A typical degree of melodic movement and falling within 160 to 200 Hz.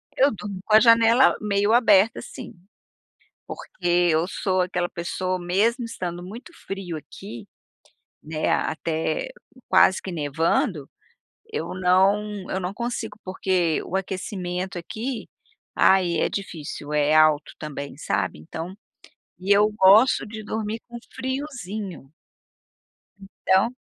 Yes: average, 3.8 semitones; high, 190 Hz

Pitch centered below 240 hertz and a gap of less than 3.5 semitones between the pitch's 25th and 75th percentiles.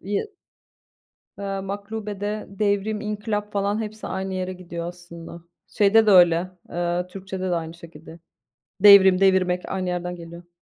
Yes: high, 190 Hz; narrow, 2.6 semitones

